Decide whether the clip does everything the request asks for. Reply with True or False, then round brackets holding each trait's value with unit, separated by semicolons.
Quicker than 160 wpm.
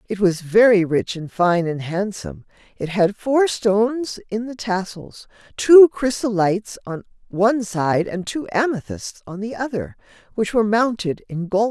False (155 wpm)